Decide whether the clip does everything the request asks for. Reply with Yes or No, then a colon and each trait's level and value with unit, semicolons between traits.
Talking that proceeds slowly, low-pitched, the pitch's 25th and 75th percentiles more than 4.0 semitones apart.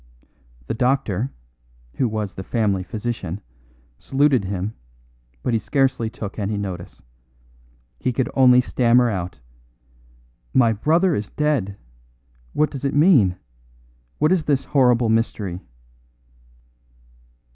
Yes: slow, 115 wpm; low, 115 Hz; average, 5.0 semitones